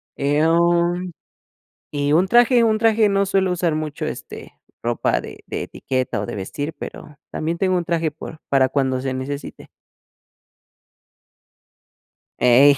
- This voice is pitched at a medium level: Yes, medium, 160 Hz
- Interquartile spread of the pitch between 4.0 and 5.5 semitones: Yes, average, 4.7 semitones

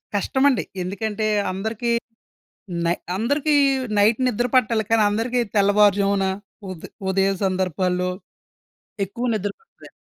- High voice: Yes, high, 205 Hz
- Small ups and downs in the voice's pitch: No, average, 3.4 semitones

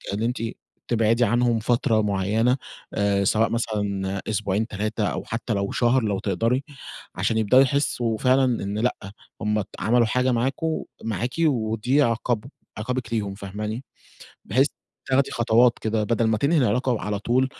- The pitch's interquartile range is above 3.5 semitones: No, average, 2.8 semitones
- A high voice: No, low, 115 Hz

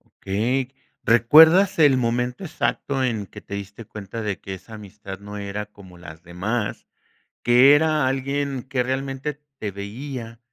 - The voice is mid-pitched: No, low, 115 Hz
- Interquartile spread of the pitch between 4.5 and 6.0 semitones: Yes, average, 5.0 semitones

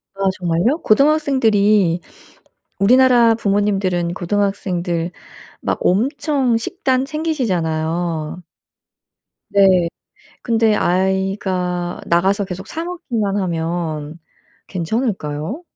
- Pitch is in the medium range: No, high, 195 Hz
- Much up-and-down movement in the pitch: No, average, 5.0 semitones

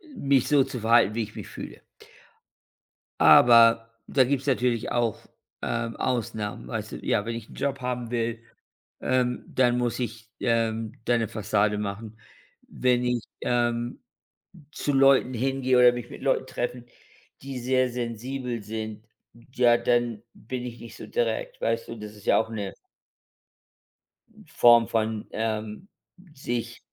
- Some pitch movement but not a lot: No, narrow, 2.0 semitones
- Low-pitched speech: Yes, low, 120 Hz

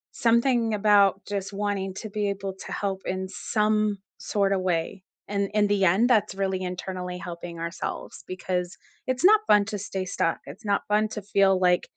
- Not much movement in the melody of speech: Yes, narrow, 2.1 semitones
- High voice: Yes, high, 195 Hz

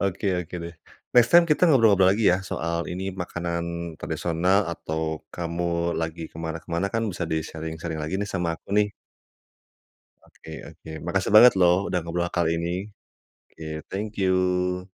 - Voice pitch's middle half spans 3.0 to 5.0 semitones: No, narrow, 2.5 semitones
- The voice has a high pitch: No, very low, 85 Hz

